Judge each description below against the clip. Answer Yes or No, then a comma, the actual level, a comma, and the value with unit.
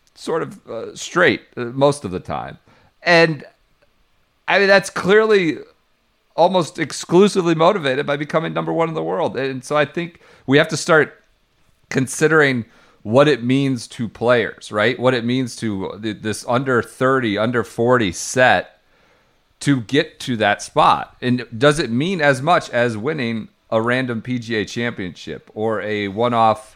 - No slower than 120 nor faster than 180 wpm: Yes, average, 155 wpm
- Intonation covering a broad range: Yes, wide, 5.7 semitones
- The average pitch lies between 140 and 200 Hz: No, low, 130 Hz